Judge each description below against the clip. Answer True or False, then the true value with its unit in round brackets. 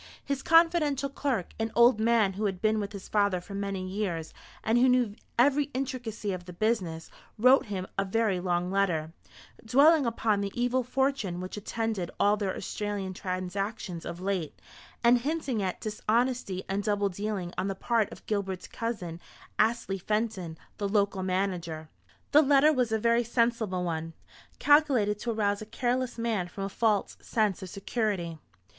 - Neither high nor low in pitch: False (210 Hz)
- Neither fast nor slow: True (165 wpm)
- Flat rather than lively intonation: False (4.0 semitones)